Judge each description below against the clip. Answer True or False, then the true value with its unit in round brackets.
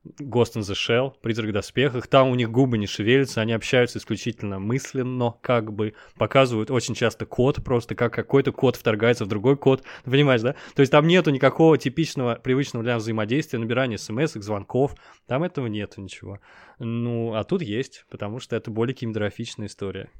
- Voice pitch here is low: True (120 Hz)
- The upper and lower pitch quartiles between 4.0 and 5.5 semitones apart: False (3.3 semitones)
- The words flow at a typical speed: False (180 wpm)